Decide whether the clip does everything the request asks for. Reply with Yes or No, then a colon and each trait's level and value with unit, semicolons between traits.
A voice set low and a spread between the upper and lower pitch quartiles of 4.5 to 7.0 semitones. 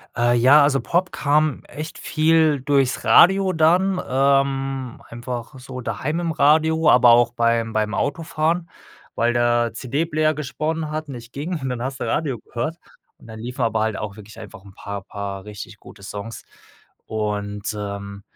Yes: low, 130 Hz; wide, 5.4 semitones